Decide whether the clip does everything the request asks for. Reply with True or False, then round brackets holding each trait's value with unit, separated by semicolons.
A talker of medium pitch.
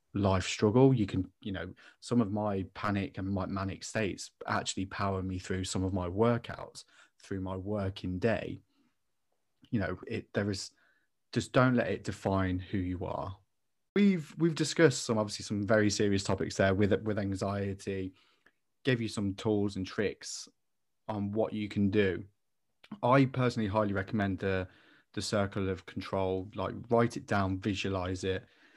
False (100 Hz)